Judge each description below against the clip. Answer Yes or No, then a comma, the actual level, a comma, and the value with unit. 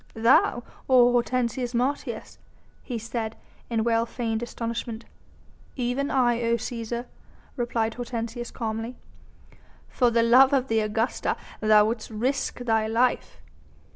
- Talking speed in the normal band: No, slow, 115 wpm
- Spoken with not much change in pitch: Yes, narrow, 1.5 semitones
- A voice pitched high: Yes, high, 235 Hz